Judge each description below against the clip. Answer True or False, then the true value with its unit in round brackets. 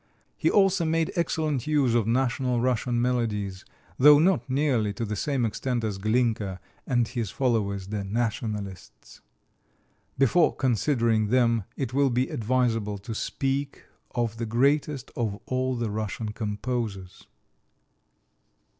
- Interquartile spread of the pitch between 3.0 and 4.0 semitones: True (3.7 semitones)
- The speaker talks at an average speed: False (130 wpm)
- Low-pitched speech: True (120 Hz)